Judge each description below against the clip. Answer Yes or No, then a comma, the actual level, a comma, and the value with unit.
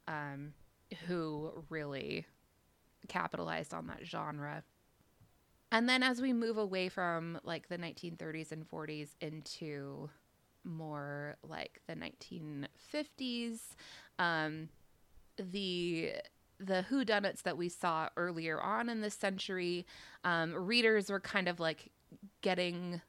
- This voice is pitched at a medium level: Yes, medium, 175 Hz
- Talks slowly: Yes, slow, 110 wpm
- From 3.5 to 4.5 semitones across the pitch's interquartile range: Yes, average, 4.1 semitones